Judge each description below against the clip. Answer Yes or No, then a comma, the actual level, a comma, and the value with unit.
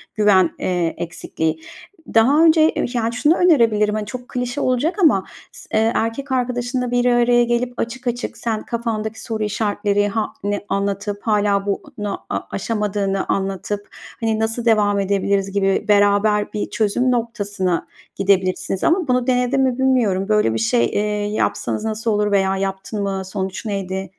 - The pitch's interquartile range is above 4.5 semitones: No, average, 3.4 semitones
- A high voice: Yes, high, 210 Hz